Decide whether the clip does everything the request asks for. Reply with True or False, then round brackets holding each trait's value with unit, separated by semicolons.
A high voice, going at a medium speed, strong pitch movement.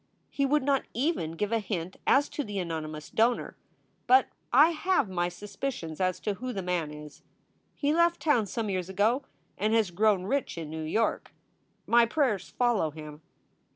True (210 Hz; 175 wpm; 6.9 semitones)